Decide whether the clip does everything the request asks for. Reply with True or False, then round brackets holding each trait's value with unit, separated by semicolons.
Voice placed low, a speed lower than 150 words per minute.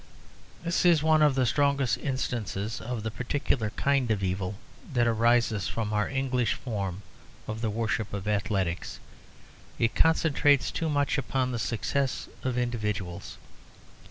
True (120 Hz; 140 wpm)